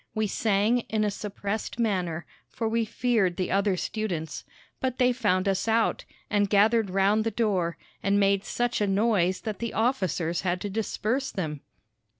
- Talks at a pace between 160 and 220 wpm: Yes, average, 165 wpm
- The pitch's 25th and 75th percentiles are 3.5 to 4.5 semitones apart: No, average, 3.0 semitones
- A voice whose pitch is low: No, high, 205 Hz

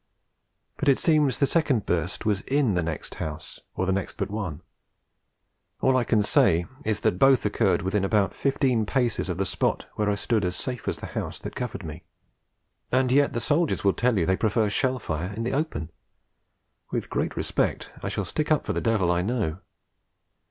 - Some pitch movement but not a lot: No, wide, 5.7 semitones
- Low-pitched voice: Yes, low, 105 Hz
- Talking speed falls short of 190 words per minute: No, average, 200 wpm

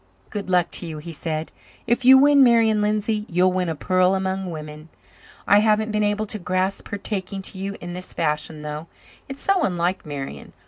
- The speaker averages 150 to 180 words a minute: No, average, 195 wpm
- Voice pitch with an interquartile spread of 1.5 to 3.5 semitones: No, average, 4.0 semitones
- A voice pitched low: No, high, 190 Hz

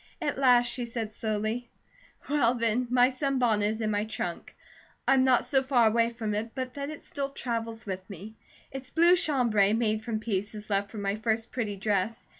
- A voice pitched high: Yes, high, 230 Hz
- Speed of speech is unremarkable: Yes, average, 190 wpm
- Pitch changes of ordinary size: Yes, average, 3.1 semitones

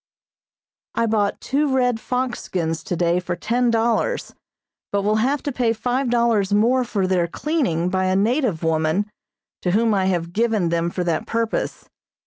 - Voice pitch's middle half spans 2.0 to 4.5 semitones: No, average, 5.0 semitones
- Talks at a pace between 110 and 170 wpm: Yes, average, 165 wpm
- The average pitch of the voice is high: Yes, high, 215 Hz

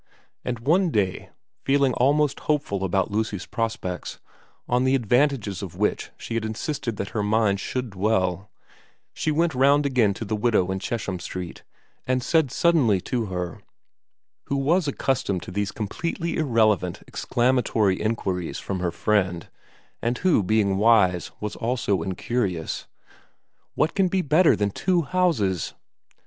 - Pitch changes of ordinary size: No, wide, 5.9 semitones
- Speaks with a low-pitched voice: Yes, low, 110 Hz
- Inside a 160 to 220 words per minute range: No, average, 145 wpm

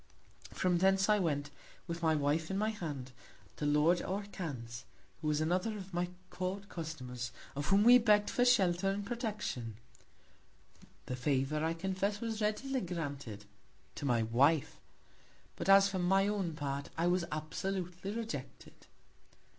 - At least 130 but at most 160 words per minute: Yes, average, 145 wpm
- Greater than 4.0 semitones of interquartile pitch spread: Yes, average, 5.2 semitones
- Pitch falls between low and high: Yes, medium, 175 Hz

